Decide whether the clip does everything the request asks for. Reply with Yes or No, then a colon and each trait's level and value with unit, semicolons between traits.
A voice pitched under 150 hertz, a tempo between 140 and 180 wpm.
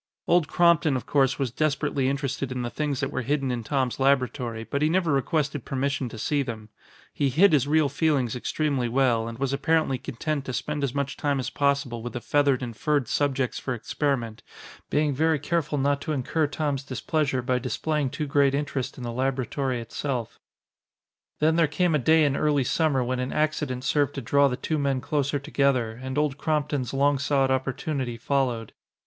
No: medium, 140 Hz; average, 190 wpm